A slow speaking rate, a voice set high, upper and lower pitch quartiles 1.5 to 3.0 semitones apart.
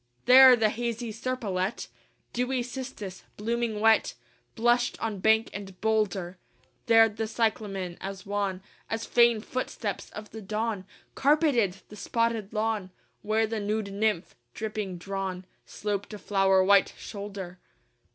Yes: slow, 130 wpm; high, 215 Hz; average, 2.7 semitones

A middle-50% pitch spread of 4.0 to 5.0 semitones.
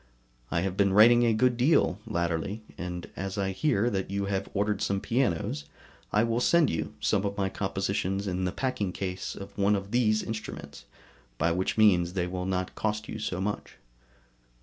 No: average, 2.8 semitones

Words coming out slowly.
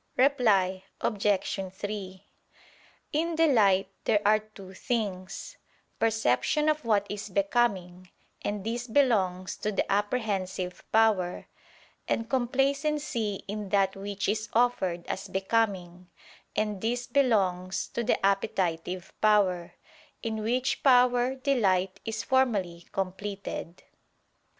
Yes: slow, 105 wpm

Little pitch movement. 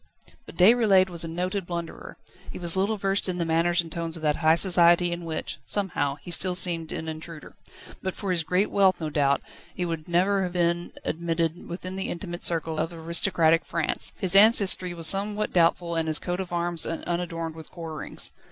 Yes: narrow, 2.1 semitones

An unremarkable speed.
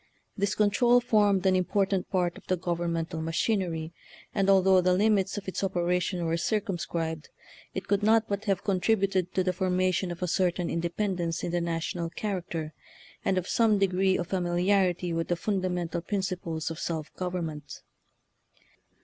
Yes: average, 165 wpm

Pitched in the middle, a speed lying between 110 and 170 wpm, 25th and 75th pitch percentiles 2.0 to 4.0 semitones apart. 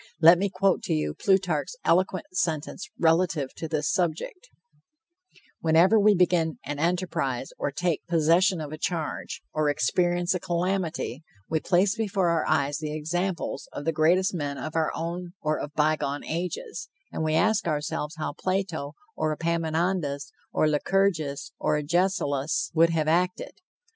Yes: medium, 165 Hz; average, 150 wpm; average, 3.0 semitones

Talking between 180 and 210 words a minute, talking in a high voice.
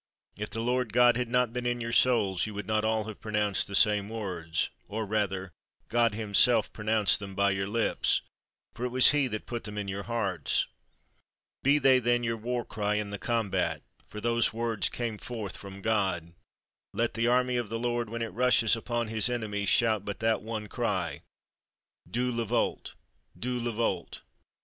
No: average, 190 wpm; low, 110 Hz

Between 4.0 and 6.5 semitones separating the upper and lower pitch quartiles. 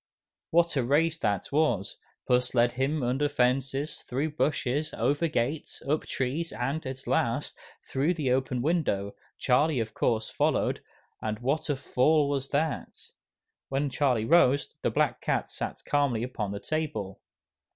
No: average, 3.6 semitones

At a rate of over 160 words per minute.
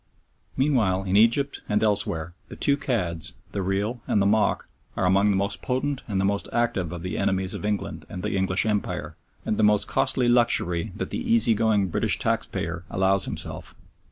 Yes: average, 185 wpm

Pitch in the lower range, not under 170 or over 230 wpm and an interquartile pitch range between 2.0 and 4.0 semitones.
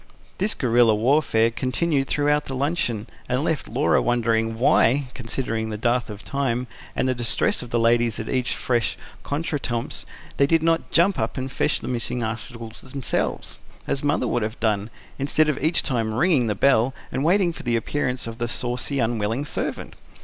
Yes: low, 125 Hz; average, 175 wpm; average, 3.7 semitones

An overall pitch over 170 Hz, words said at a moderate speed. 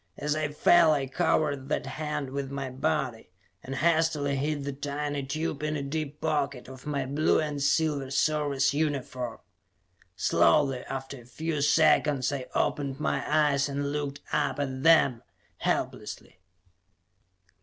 No: medium, 145 Hz; average, 145 wpm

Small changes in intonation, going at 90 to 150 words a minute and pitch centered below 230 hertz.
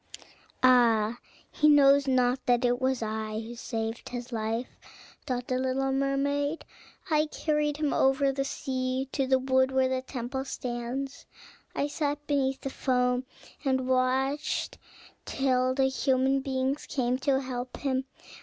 No: narrow, 1.7 semitones; average, 145 wpm; very high, 260 Hz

